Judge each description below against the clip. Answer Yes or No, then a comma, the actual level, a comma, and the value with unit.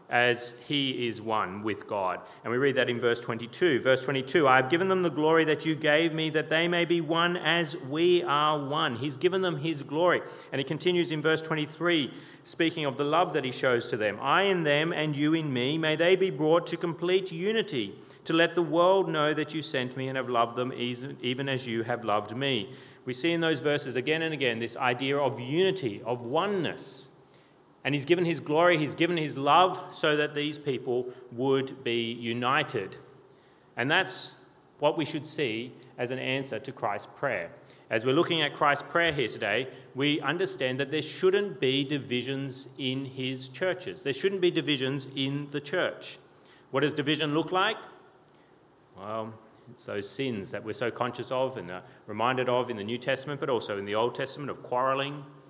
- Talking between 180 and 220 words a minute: Yes, average, 200 wpm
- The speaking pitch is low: No, medium, 145 Hz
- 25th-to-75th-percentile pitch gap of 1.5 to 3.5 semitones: No, average, 4.1 semitones